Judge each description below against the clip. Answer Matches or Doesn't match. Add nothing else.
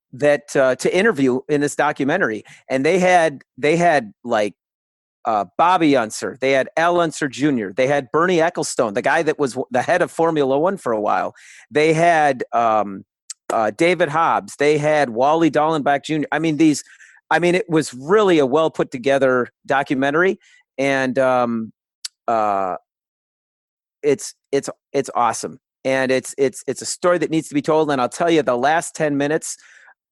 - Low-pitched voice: Doesn't match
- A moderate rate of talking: Matches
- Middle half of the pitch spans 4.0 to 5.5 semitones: Doesn't match